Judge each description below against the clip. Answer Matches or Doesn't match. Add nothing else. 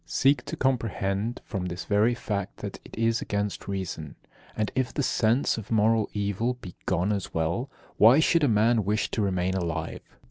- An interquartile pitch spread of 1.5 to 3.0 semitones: Doesn't match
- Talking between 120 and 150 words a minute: Doesn't match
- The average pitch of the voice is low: Matches